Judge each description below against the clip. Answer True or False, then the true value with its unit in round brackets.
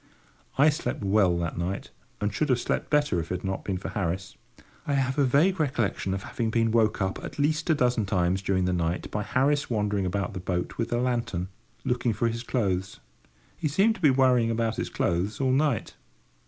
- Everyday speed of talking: False (210 wpm)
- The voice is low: True (110 Hz)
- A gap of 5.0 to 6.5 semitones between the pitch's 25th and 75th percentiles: True (5.5 semitones)